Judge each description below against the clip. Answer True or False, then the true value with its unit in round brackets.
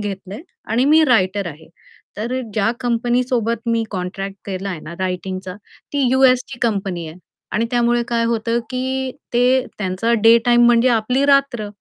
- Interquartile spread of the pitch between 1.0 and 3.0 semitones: False (4.0 semitones)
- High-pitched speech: True (230 Hz)